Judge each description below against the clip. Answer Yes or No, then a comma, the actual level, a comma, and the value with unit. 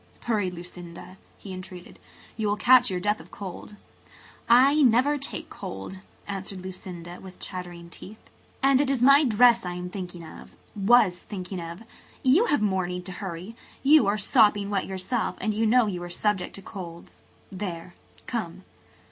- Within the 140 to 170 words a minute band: Yes, average, 160 wpm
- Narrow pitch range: No, average, 4.3 semitones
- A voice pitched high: Yes, high, 195 Hz